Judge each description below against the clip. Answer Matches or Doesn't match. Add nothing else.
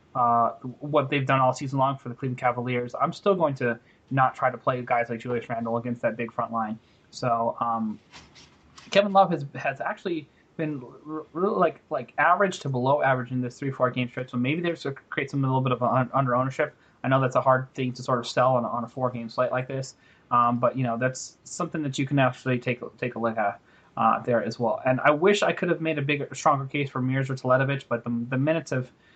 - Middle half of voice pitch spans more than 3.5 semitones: Doesn't match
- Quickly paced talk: Matches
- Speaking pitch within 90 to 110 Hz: Doesn't match